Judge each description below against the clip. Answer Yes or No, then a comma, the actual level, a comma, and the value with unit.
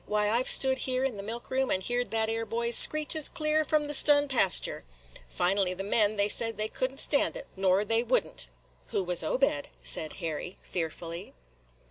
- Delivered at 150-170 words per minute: No, average, 200 wpm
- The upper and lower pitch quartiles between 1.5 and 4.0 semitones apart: No, wide, 5.6 semitones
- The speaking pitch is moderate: No, high, 225 Hz